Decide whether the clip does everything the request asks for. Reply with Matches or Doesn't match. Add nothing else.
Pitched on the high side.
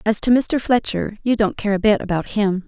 Matches